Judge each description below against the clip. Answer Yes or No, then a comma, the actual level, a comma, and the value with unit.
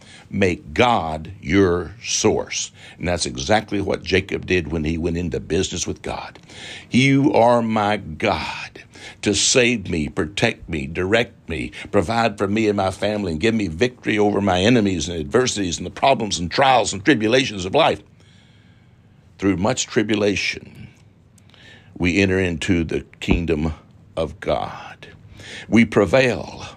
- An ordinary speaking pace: Yes, average, 145 wpm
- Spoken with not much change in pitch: No, average, 4.2 semitones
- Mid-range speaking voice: No, low, 100 Hz